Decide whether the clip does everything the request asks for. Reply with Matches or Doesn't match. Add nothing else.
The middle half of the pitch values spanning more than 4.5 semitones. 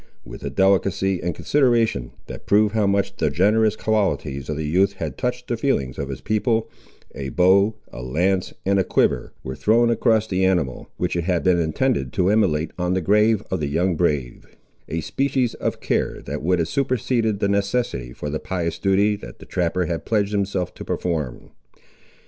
Matches